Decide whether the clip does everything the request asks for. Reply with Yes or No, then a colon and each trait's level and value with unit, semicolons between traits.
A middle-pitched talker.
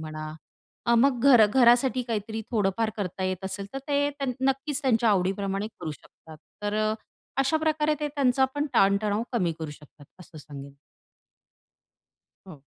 No: high, 215 Hz